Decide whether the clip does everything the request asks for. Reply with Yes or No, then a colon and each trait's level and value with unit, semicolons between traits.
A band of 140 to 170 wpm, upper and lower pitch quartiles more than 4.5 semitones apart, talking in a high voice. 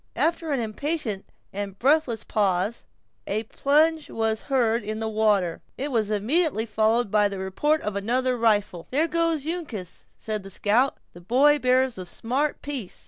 Yes: average, 165 wpm; wide, 5.5 semitones; high, 225 Hz